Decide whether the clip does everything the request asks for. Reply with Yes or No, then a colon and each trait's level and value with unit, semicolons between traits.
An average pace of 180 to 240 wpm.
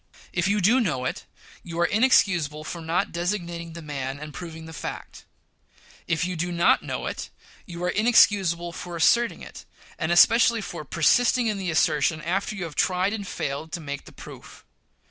Yes: average, 185 wpm